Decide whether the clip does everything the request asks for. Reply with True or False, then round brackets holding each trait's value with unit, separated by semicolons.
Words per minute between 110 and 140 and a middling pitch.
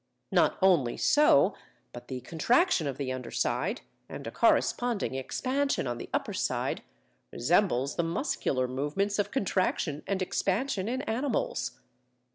True (135 wpm; 180 Hz)